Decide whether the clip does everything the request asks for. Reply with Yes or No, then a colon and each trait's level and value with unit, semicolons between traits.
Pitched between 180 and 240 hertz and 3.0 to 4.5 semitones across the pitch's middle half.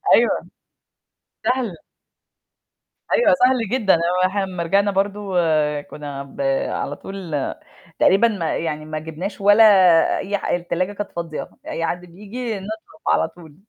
Yes: high, 190 Hz; average, 3.6 semitones